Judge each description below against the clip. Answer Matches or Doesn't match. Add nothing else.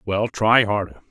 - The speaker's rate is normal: Matches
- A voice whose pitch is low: Matches